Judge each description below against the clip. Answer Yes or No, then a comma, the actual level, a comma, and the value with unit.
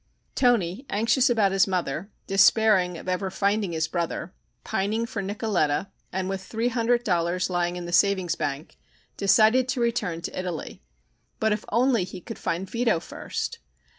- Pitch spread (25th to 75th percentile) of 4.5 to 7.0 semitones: No, average, 4.0 semitones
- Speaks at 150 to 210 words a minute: Yes, average, 160 wpm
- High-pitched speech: Yes, high, 195 Hz